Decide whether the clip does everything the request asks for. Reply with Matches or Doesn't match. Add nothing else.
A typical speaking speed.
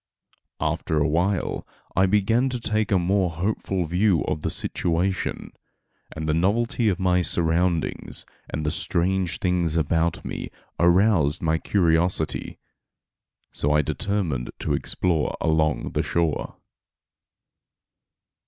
Doesn't match